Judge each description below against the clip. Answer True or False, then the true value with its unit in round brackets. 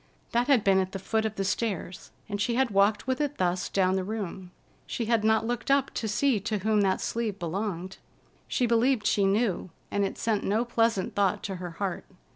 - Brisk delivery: True (215 wpm)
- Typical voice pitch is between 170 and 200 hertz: False (210 Hz)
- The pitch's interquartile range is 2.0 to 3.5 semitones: True (3.2 semitones)